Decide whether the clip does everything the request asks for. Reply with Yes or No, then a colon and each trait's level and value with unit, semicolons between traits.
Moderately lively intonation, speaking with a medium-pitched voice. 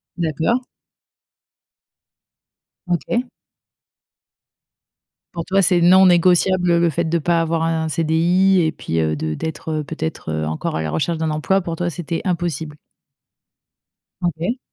No: narrow, 2.2 semitones; medium, 165 Hz